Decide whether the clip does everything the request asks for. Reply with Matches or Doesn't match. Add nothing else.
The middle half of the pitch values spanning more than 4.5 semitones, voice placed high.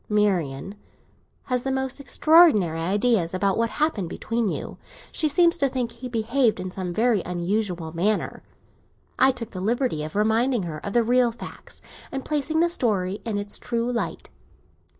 Matches